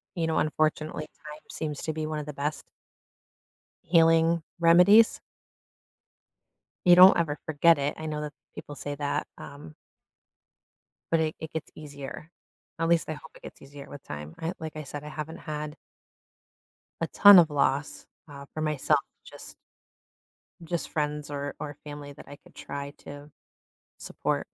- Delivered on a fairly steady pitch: Yes, narrow, 2.0 semitones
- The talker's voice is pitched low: No, medium, 150 Hz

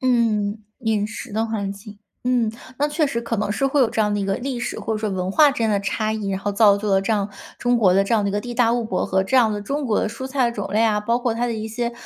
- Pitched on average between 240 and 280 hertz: No, high, 220 Hz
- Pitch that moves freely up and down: No, average, 2.9 semitones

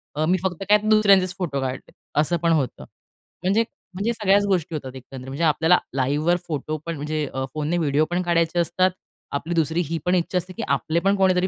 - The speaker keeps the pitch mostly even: No, average, 3.5 semitones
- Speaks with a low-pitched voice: No, medium, 170 Hz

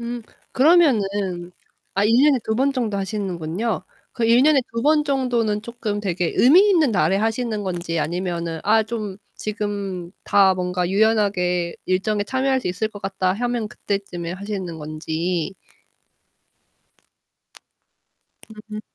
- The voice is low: No, high, 205 Hz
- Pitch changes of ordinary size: Yes, average, 4.5 semitones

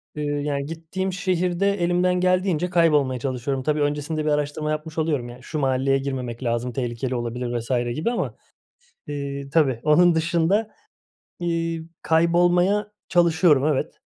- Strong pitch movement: No, average, 4.3 semitones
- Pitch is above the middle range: No, medium, 155 Hz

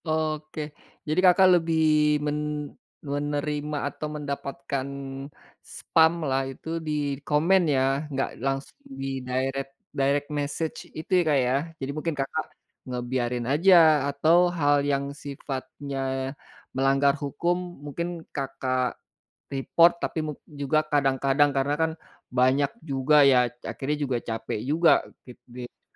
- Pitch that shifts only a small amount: Yes, narrow, 2.3 semitones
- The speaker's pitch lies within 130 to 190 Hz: Yes, medium, 140 Hz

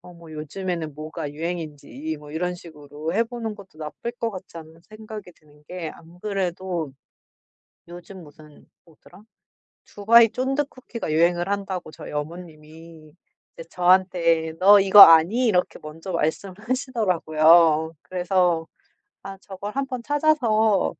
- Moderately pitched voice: Yes, medium, 175 Hz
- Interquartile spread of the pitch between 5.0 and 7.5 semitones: No, average, 4.1 semitones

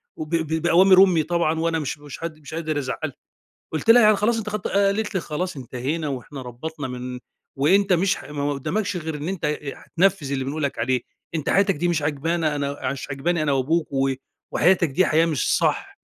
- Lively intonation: No, average, 4.0 semitones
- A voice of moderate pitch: Yes, medium, 155 Hz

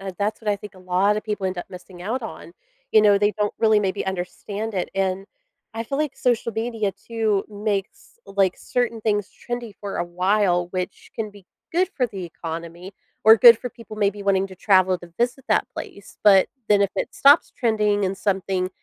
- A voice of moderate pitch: No, high, 205 Hz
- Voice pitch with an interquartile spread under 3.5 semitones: Yes, average, 2.7 semitones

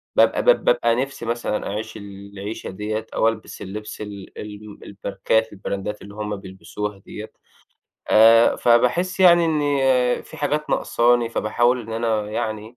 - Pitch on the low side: Yes, low, 110 Hz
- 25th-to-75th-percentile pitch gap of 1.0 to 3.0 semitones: Yes, average, 2.7 semitones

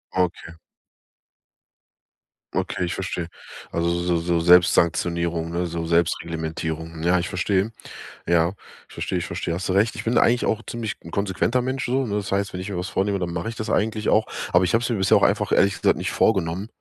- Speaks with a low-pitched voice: Yes, very low, 90 Hz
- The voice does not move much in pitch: No, average, 3.4 semitones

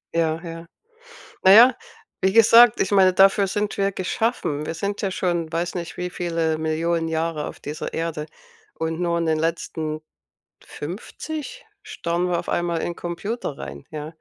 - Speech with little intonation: No, average, 3.2 semitones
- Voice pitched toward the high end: No, medium, 170 Hz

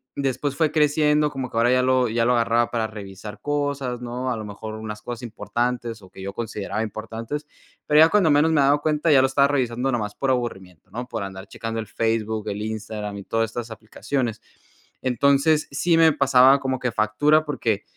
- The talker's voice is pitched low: Yes, low, 120 Hz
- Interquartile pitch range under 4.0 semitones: No, average, 4.3 semitones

